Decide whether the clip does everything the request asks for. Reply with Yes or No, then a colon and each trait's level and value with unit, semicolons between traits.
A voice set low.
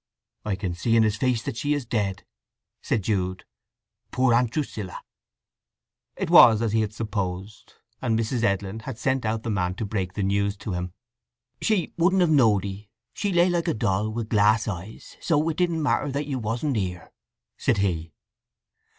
Yes: low, 110 Hz